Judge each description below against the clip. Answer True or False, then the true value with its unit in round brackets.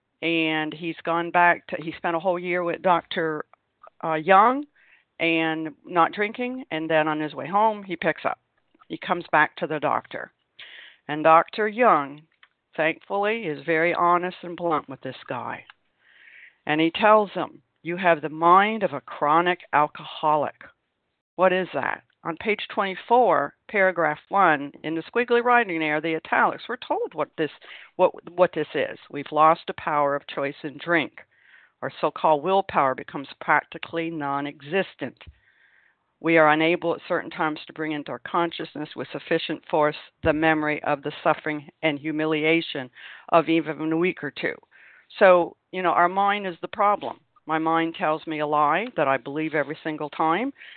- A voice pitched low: False (165 Hz)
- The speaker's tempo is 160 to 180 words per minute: True (170 wpm)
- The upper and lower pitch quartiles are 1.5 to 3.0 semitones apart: True (2.7 semitones)